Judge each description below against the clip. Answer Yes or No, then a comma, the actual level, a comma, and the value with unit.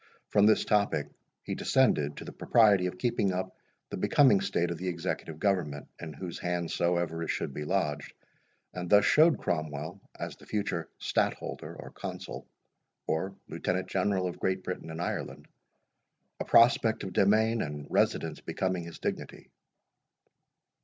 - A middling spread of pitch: Yes, average, 3.5 semitones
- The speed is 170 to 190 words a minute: No, average, 155 wpm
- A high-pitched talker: No, very low, 90 Hz